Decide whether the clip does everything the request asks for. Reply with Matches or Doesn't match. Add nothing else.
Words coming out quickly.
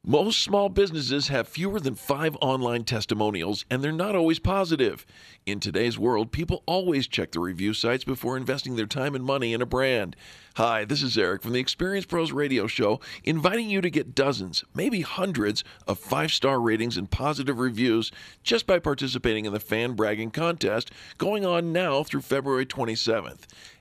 Doesn't match